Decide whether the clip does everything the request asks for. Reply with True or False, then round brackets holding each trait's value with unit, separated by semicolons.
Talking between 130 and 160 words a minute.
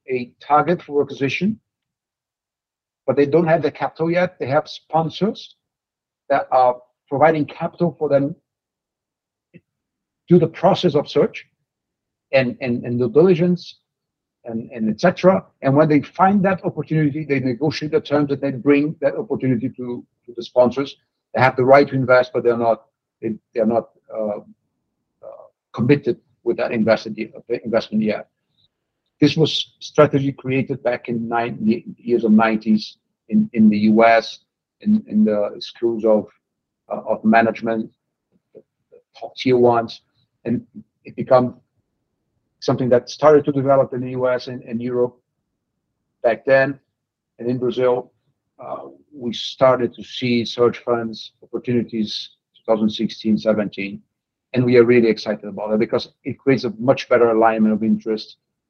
True (145 wpm)